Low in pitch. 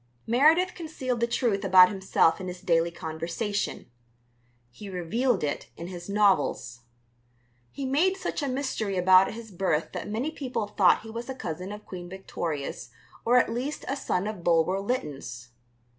No: high, 200 Hz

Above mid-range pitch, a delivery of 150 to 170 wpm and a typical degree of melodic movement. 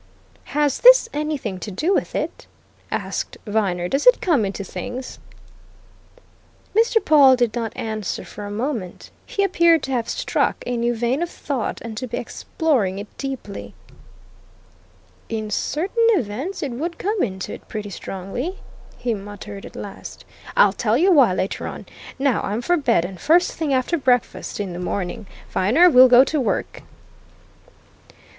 No: high, 245 Hz; average, 160 wpm; wide, 6.7 semitones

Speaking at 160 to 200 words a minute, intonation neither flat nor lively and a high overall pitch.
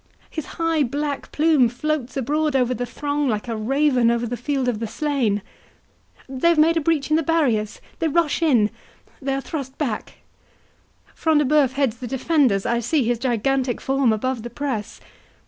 Yes: average, 165 wpm; average, 4.0 semitones; very high, 270 Hz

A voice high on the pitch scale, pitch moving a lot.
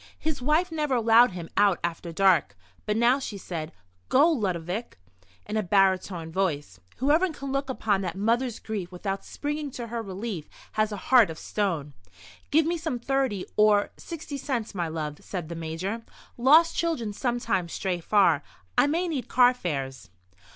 Yes: high, 210 Hz; wide, 6.9 semitones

